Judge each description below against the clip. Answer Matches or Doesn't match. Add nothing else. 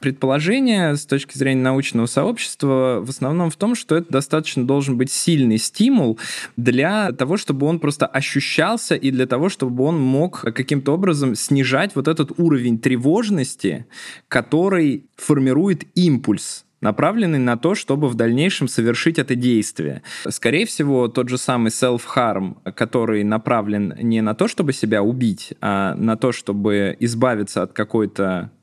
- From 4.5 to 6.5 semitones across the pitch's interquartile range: Matches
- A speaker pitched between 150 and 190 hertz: Doesn't match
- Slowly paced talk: Doesn't match